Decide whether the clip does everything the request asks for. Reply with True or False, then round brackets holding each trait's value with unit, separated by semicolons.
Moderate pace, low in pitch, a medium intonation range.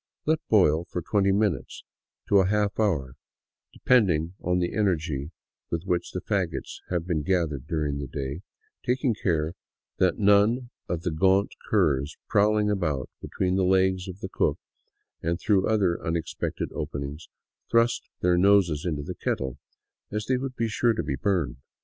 True (165 wpm; 90 Hz; 4.6 semitones)